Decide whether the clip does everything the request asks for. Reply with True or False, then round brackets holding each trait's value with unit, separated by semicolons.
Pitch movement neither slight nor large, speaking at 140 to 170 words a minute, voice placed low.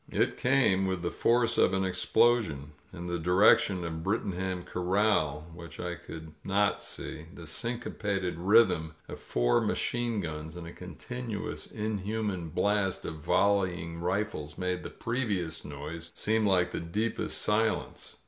True (4.1 semitones; 150 wpm; 95 Hz)